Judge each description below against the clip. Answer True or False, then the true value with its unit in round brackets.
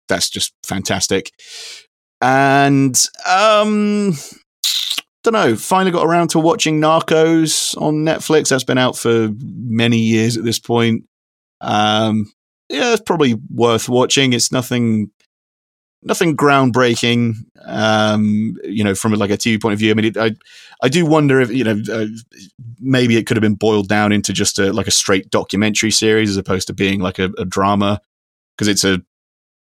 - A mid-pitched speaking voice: False (115 Hz)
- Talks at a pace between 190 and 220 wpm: False (165 wpm)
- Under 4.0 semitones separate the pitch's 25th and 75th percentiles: False (4.6 semitones)